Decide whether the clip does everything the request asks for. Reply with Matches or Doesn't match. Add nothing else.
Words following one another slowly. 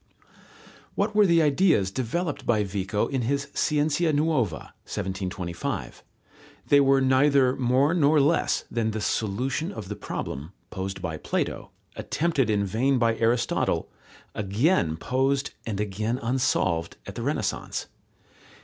Matches